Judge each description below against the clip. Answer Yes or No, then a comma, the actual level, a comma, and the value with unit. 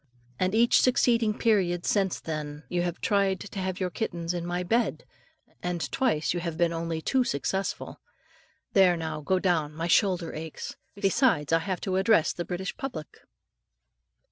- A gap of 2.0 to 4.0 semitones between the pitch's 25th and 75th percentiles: Yes, average, 3.1 semitones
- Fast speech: No, average, 165 wpm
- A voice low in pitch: No, medium, 180 Hz